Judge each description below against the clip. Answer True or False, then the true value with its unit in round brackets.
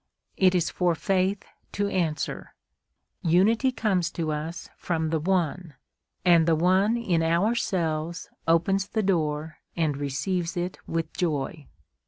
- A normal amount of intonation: True (3.0 semitones)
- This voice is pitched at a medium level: True (170 Hz)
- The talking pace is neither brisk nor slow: False (130 wpm)